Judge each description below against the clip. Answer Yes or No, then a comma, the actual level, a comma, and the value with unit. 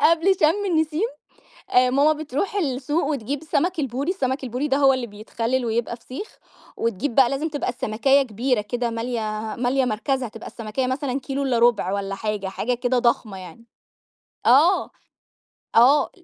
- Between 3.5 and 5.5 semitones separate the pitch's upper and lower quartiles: Yes, average, 3.8 semitones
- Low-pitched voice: No, very high, 255 Hz